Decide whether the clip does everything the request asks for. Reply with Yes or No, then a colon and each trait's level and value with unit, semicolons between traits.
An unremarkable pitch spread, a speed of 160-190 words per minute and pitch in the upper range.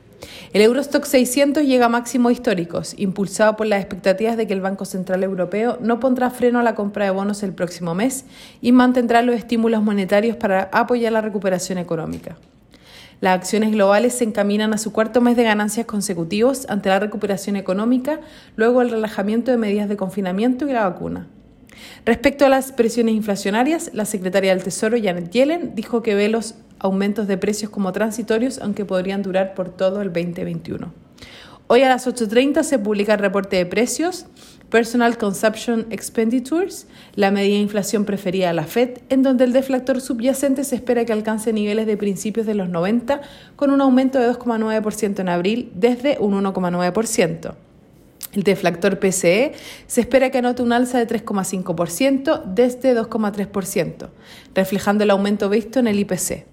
Yes: average, 3.6 semitones; average, 165 wpm; high, 220 Hz